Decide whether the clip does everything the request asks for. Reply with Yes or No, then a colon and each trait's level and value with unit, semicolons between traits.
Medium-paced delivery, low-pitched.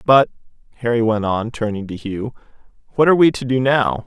Yes: average, 190 wpm; low, 115 Hz